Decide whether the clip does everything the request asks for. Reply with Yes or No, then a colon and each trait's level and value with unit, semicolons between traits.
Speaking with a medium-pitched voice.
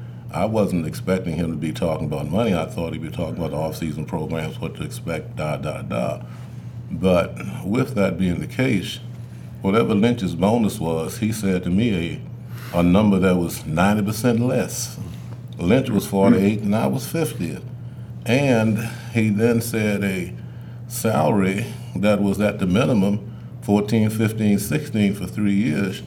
No: low, 105 Hz